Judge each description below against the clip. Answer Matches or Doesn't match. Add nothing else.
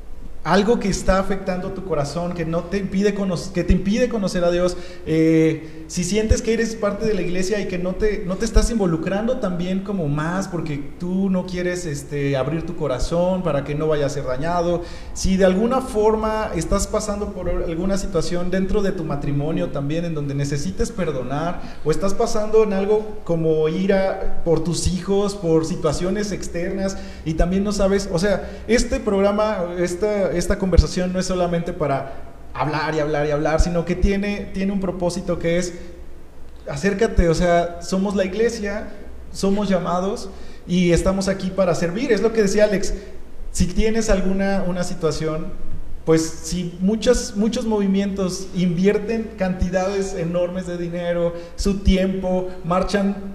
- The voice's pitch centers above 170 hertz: Matches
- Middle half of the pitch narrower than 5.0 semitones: Matches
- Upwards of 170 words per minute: Doesn't match